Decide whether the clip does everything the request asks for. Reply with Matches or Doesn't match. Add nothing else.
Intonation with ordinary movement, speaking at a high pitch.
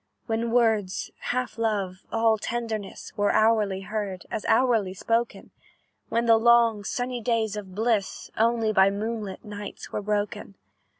Doesn't match